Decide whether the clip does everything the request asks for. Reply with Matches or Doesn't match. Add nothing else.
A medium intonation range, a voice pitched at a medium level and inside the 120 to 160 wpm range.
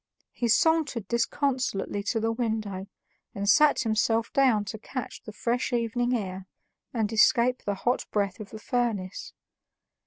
Doesn't match